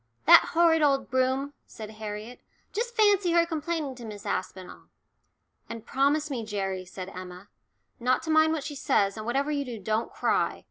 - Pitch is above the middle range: Yes, very high, 255 Hz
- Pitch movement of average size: No, wide, 6.7 semitones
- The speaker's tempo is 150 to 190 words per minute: Yes, average, 175 wpm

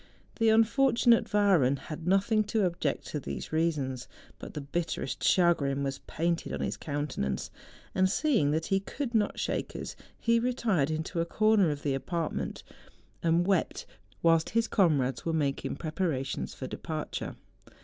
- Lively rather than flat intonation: Yes, wide, 6.0 semitones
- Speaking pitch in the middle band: Yes, medium, 165 Hz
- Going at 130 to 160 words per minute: Yes, average, 155 wpm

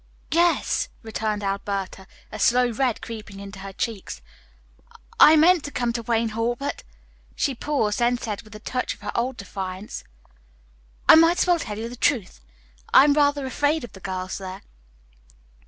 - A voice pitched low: No, high, 230 Hz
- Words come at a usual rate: Yes, average, 175 wpm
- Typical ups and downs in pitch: No, wide, 5.8 semitones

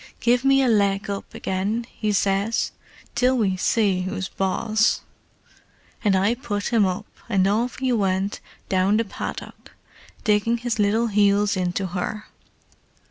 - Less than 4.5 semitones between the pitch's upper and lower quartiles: Yes, average, 2.9 semitones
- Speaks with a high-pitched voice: Yes, high, 205 Hz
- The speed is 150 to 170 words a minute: No, average, 140 wpm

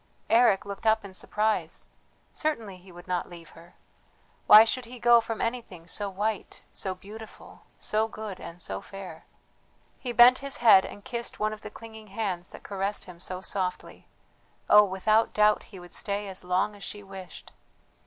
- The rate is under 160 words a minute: No, average, 175 wpm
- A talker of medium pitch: No, high, 205 Hz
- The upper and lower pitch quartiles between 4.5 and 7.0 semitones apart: No, average, 2.9 semitones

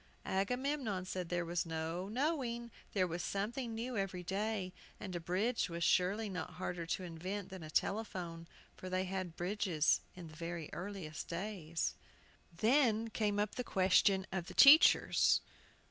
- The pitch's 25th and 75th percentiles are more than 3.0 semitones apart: Yes, average, 3.8 semitones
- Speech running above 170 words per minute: No, average, 155 wpm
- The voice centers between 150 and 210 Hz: Yes, high, 190 Hz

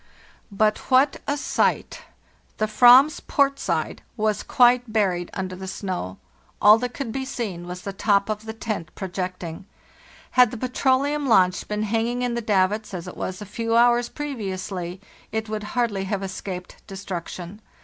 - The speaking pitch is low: No, high, 215 Hz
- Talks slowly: No, average, 165 wpm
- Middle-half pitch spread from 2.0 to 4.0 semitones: No, average, 4.4 semitones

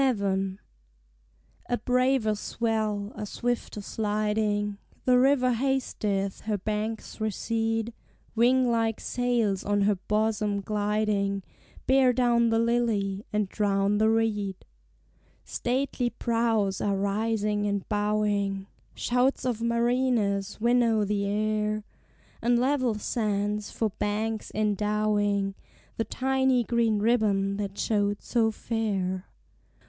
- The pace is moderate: No, slow, 110 wpm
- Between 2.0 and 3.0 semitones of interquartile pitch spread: Yes, narrow, 2.5 semitones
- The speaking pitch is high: Yes, high, 215 Hz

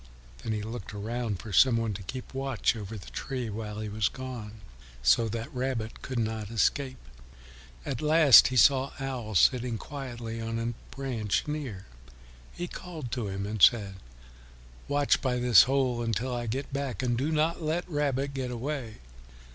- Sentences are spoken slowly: No, average, 170 wpm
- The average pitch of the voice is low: Yes, low, 120 Hz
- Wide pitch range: No, average, 3.6 semitones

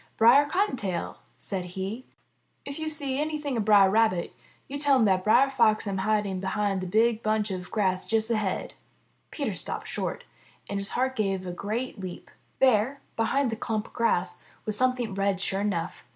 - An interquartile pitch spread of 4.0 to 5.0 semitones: Yes, average, 4.7 semitones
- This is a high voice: Yes, high, 215 Hz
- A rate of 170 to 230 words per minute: Yes, average, 180 wpm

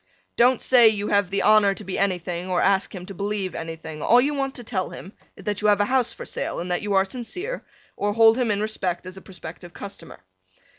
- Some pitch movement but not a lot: Yes, average, 3.3 semitones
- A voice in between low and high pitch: No, high, 200 Hz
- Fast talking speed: Yes, fast, 240 wpm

